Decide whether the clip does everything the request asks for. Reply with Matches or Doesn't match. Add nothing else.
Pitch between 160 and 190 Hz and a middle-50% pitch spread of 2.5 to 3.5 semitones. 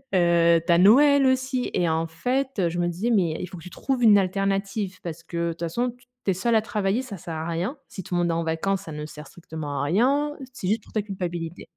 Doesn't match